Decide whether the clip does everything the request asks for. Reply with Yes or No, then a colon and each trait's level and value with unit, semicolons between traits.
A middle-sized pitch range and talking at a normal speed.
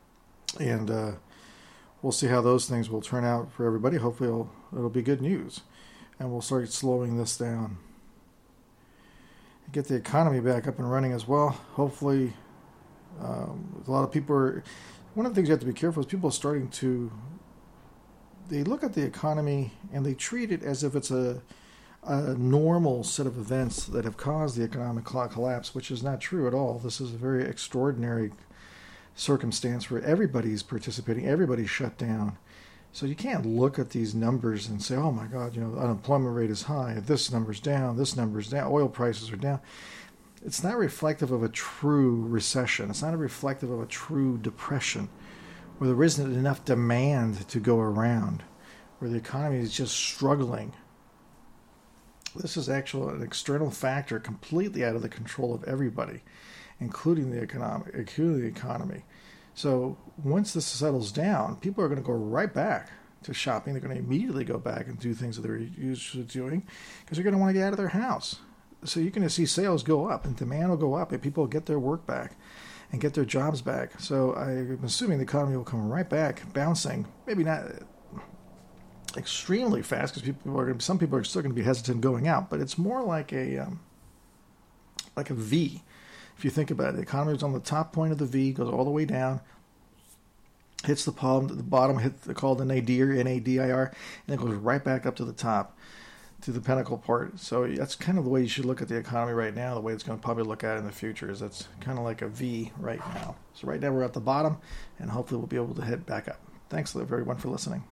No: average, 3.7 semitones; fast, 210 wpm